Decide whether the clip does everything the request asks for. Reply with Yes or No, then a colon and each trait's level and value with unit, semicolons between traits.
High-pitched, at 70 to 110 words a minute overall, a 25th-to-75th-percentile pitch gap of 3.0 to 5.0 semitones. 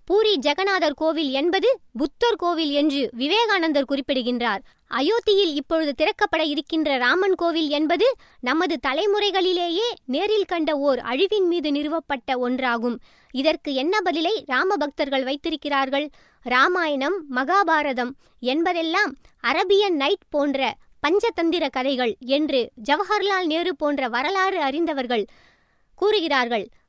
No: very high, 315 Hz; average, 105 wpm; wide, 5.4 semitones